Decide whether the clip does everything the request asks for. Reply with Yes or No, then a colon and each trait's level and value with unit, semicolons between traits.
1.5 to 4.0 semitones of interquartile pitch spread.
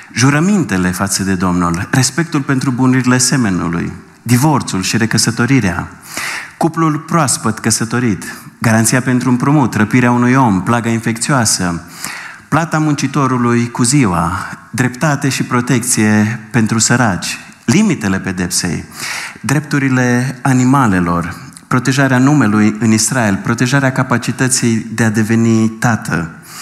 Yes: average, 3.4 semitones